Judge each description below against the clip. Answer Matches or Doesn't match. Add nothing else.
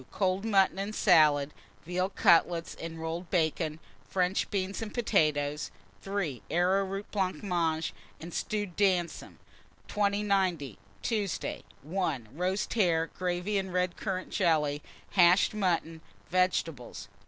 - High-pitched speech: Doesn't match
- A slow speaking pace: Matches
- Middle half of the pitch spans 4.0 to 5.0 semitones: Doesn't match